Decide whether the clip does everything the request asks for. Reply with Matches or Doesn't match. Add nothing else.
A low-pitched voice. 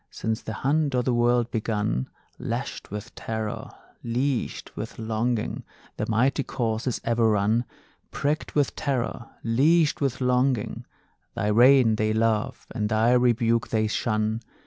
Matches